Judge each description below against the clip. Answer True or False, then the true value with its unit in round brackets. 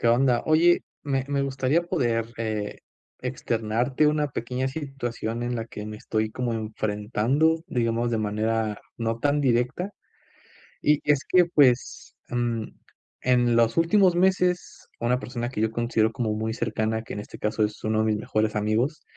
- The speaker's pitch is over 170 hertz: False (120 Hz)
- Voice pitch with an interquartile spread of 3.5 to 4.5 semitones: True (3.9 semitones)